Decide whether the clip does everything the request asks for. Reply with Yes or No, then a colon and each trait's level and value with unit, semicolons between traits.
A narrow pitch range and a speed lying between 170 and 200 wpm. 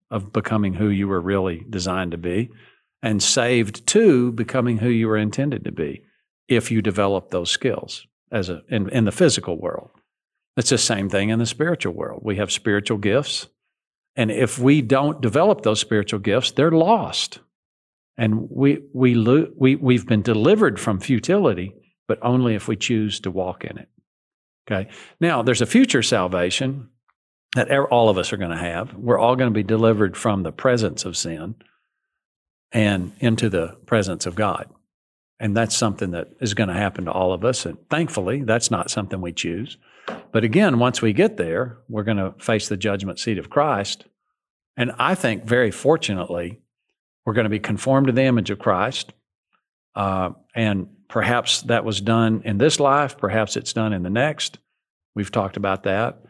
No: average, 3.6 semitones; average, 180 wpm